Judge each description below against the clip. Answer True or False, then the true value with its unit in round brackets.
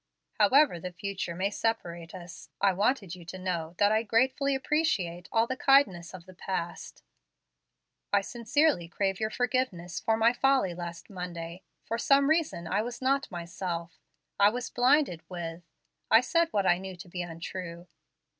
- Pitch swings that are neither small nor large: False (6.0 semitones)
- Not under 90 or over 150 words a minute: False (165 wpm)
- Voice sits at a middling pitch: False (195 Hz)